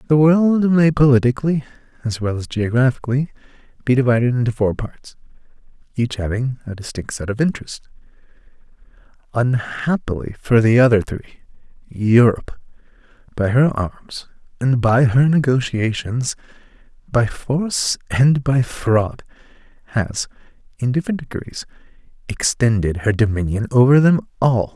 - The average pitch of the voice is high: No, low, 125 Hz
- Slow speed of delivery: Yes, slow, 115 wpm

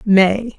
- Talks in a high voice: Yes, high, 205 Hz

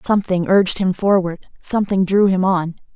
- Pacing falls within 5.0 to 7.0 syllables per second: Yes, 5.4 syllables/s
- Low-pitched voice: No, high, 190 Hz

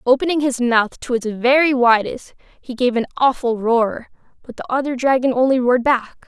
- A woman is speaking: Yes, female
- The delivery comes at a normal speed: Yes, average, 180 wpm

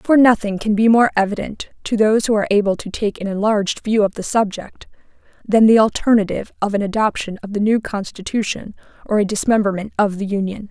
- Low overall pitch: No, high, 210 Hz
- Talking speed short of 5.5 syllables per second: No, 6.0 syllables/s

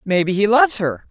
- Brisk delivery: Yes, fast, 220 wpm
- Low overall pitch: No, high, 215 Hz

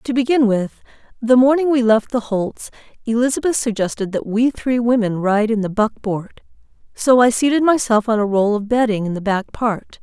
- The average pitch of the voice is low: No, high, 230 Hz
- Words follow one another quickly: No, average, 190 wpm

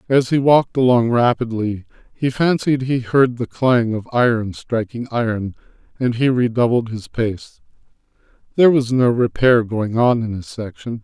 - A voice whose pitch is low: Yes, low, 120 Hz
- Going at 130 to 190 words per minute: Yes, average, 160 wpm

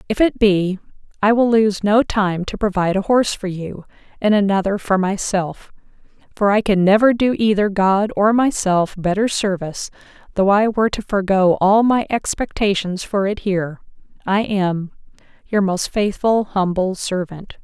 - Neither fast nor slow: Yes, average, 160 wpm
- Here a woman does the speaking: Yes, female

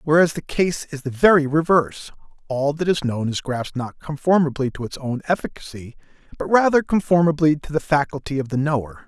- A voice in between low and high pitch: Yes, medium, 145 Hz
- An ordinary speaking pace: Yes, average, 185 wpm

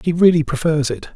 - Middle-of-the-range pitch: Yes, medium, 155 Hz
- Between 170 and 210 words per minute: Yes, fast, 205 wpm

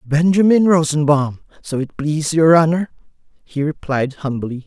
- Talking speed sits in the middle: No, slow, 130 wpm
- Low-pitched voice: No, medium, 155 Hz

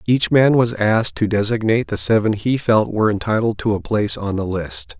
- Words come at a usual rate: No, fast, 215 wpm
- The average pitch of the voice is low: Yes, low, 110 Hz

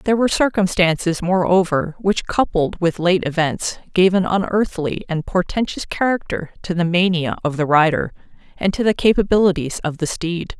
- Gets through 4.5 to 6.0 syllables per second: Yes, 5.1 syllables/s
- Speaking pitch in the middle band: Yes, medium, 180 Hz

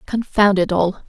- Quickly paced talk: No, average, 165 wpm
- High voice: Yes, high, 195 Hz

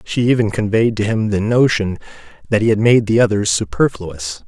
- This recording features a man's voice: Yes, male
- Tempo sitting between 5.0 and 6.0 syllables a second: Yes, 5.2 syllables/s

